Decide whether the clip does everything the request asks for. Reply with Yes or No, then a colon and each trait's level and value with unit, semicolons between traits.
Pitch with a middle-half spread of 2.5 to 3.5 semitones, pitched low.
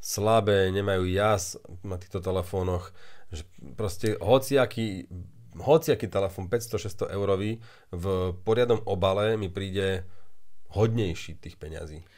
Yes: average, 2.8 semitones; very low, 95 Hz